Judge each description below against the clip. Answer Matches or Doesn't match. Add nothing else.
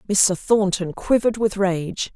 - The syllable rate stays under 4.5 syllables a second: Matches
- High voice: Matches